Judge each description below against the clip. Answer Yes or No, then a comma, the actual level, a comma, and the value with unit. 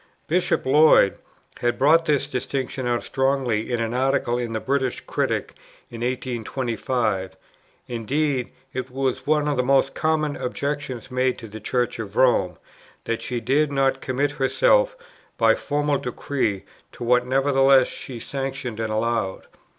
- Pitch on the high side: No, low, 130 Hz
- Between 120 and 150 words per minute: Yes, average, 145 wpm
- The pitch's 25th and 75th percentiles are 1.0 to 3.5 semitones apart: Yes, average, 2.8 semitones